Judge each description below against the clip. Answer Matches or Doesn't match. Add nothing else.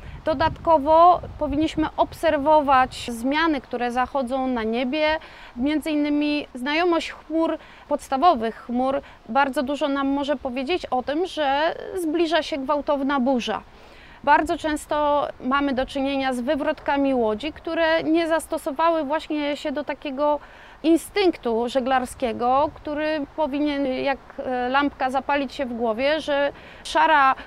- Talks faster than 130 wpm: Doesn't match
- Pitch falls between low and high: Doesn't match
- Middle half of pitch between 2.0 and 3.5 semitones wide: Matches